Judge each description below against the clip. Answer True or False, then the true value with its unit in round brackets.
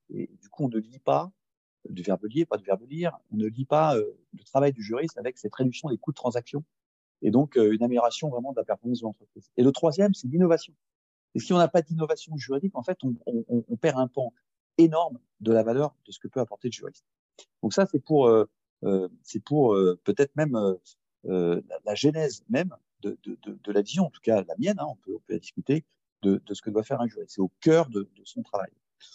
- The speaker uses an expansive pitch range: True (6.9 semitones)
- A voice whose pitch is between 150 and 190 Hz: False (135 Hz)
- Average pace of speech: False (250 wpm)